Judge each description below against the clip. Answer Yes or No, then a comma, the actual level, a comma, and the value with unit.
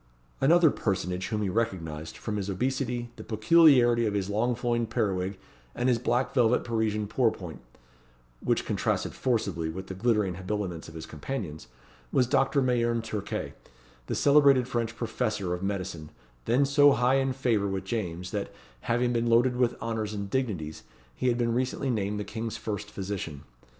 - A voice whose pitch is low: Yes, low, 110 Hz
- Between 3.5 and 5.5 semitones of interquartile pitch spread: Yes, average, 4.2 semitones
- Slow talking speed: No, average, 165 wpm